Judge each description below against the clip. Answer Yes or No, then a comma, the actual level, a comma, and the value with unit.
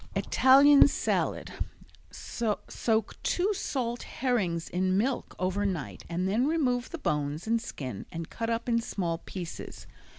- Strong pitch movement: Yes, wide, 6.0 semitones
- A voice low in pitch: No, high, 220 Hz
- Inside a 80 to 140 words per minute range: Yes, slow, 135 wpm